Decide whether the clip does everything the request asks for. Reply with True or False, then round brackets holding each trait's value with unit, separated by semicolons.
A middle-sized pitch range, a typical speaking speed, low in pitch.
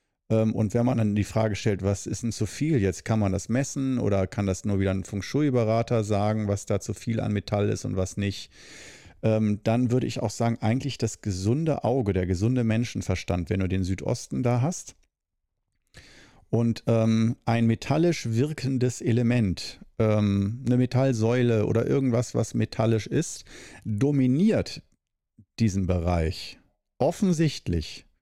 True (3.5 semitones; 150 wpm; 110 Hz)